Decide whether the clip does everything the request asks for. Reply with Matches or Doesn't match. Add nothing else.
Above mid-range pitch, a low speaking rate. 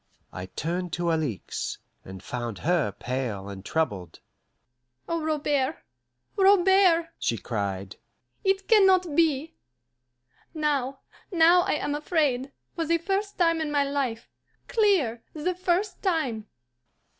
Matches